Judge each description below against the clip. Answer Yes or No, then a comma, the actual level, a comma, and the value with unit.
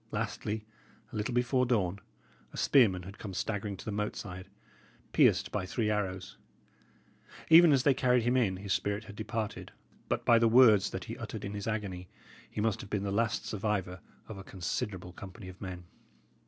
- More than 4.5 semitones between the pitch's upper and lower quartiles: No, average, 3.0 semitones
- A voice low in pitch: Yes, low, 105 Hz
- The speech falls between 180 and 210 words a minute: Yes, average, 185 wpm